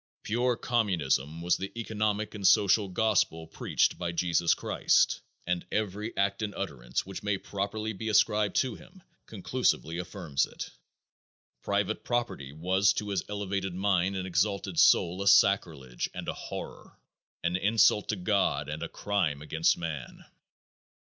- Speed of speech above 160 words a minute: No, average, 145 wpm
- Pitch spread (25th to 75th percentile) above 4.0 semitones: No, average, 3.5 semitones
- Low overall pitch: Yes, very low, 95 Hz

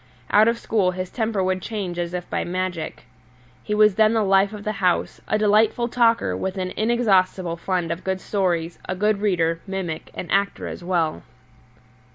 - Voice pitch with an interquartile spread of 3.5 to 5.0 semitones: No, average, 3.0 semitones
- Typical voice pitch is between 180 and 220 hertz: Yes, high, 190 Hz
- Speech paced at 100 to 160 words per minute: No, average, 180 wpm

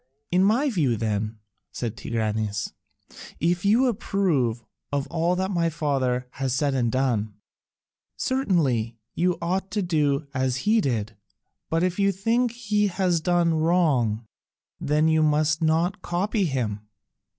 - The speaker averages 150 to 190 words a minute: No, average, 140 wpm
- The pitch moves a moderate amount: No, wide, 6.8 semitones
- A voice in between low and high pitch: Yes, medium, 160 Hz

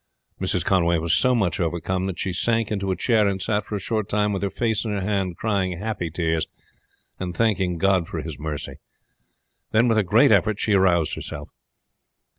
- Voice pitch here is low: Yes, very low, 95 Hz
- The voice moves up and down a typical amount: Yes, average, 3.6 semitones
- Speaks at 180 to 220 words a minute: Yes, average, 200 wpm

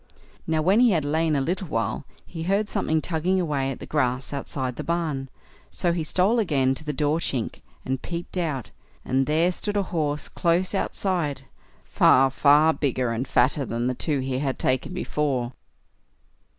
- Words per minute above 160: Yes, average, 175 wpm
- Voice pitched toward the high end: No, medium, 150 Hz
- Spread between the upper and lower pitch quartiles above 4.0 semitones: Yes, average, 4.4 semitones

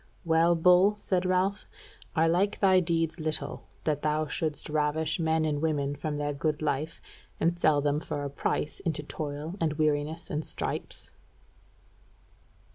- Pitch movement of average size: No, narrow, 2.1 semitones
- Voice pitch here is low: No, medium, 155 Hz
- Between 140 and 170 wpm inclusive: Yes, average, 150 wpm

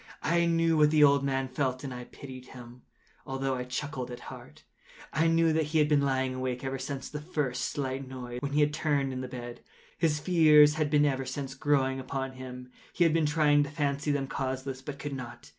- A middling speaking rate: No, fast, 215 wpm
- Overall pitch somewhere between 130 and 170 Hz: Yes, medium, 140 Hz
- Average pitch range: No, narrow, 2.3 semitones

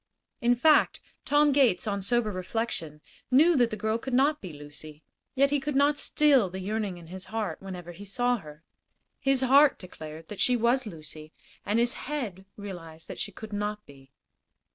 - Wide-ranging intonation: Yes, wide, 6.5 semitones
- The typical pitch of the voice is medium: No, high, 210 Hz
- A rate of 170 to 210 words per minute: Yes, average, 185 wpm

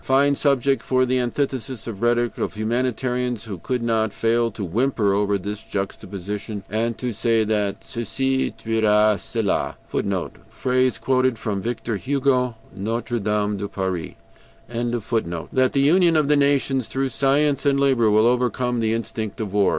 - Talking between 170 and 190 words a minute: No, average, 155 wpm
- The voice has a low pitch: Yes, low, 115 Hz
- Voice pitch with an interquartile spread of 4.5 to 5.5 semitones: No, average, 3.5 semitones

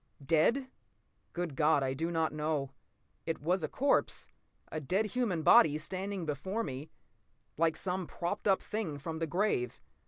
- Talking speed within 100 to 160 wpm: Yes, average, 155 wpm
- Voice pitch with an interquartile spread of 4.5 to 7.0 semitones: No, average, 3.9 semitones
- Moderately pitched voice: Yes, medium, 165 Hz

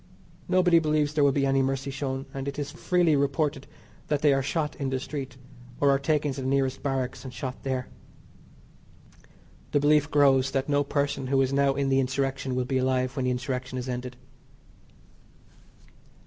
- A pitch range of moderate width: No, narrow, 1.5 semitones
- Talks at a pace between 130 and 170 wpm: No, average, 185 wpm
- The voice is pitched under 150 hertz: Yes, low, 135 Hz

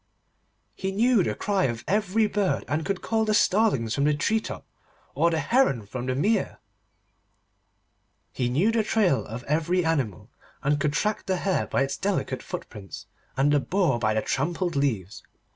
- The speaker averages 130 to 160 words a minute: No, average, 175 wpm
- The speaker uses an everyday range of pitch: No, wide, 7.5 semitones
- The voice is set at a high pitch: No, medium, 165 Hz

